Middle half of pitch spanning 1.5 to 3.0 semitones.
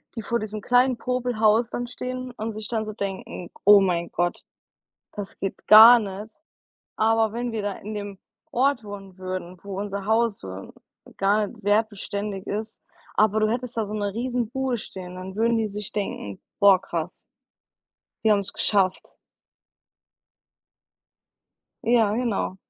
Yes: average, 2.7 semitones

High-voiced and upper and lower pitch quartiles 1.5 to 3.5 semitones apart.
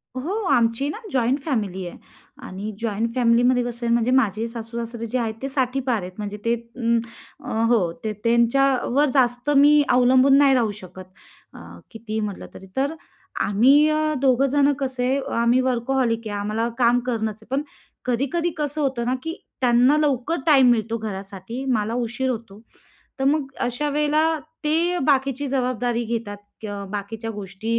Yes: high, 245 Hz; average, 3.2 semitones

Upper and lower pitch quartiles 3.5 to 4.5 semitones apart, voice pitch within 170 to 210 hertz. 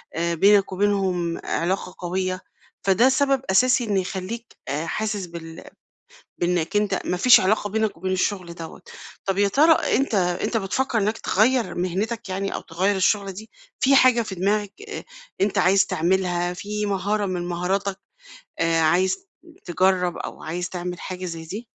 No: average, 2.9 semitones; high, 190 Hz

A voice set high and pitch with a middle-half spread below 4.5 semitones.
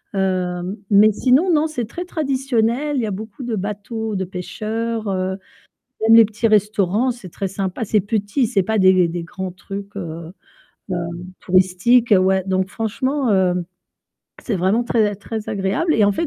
Yes: high, 210 Hz; average, 3.5 semitones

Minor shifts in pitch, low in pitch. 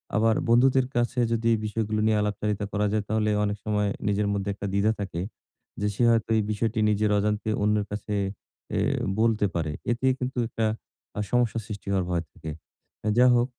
Yes: narrow, 1.8 semitones; low, 105 Hz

